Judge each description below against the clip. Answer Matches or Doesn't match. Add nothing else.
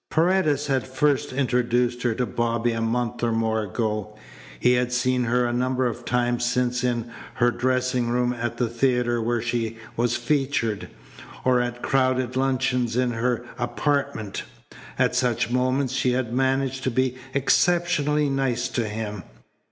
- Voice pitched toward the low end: Matches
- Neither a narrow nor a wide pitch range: Doesn't match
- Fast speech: Doesn't match